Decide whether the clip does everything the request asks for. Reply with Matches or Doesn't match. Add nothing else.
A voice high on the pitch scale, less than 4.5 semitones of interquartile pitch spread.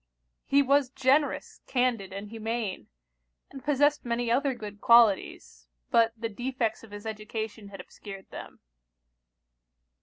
Matches